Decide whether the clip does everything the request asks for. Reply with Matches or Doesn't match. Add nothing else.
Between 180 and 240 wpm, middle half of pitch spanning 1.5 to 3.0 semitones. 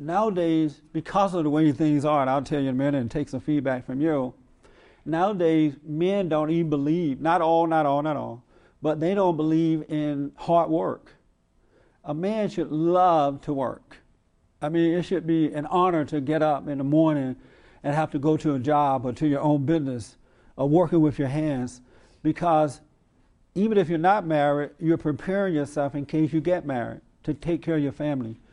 Matches